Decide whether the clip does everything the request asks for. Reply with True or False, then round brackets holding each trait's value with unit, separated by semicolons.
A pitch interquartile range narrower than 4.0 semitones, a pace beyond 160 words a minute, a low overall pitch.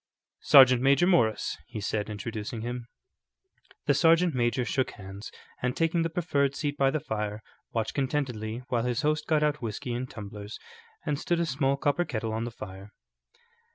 False (5.1 semitones; 170 wpm; 125 Hz)